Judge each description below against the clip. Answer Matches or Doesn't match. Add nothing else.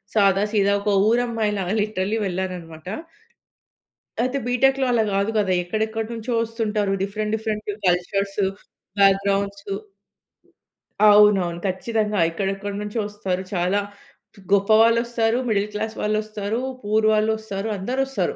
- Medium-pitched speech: Doesn't match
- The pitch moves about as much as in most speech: Doesn't match